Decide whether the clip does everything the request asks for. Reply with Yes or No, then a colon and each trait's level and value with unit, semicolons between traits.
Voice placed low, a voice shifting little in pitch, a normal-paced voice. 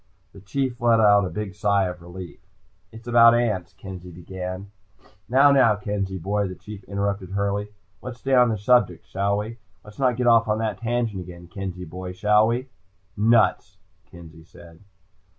No: low, 100 Hz; average, 3.9 semitones; average, 170 wpm